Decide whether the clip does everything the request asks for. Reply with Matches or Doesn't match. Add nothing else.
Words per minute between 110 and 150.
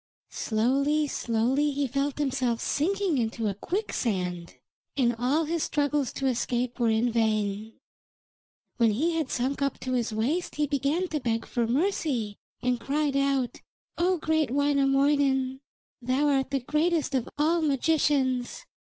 Matches